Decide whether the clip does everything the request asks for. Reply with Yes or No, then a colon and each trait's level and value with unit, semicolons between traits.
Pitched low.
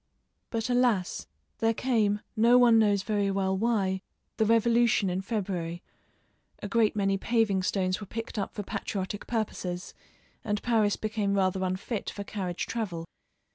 No: high, 205 Hz